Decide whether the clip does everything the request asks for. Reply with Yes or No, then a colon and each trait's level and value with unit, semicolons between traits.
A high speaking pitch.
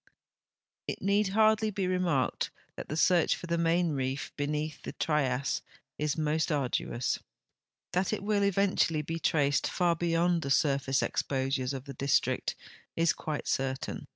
No: medium, 155 Hz